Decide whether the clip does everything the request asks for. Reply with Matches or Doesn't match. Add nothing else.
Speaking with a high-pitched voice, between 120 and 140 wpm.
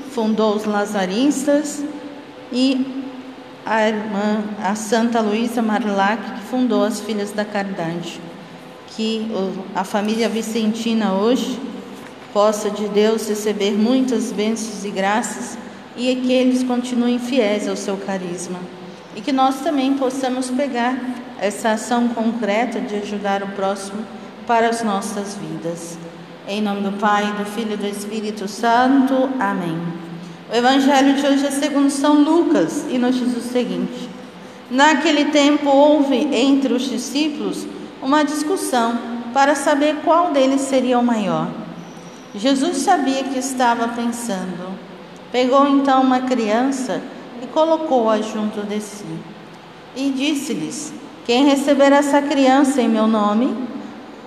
Matches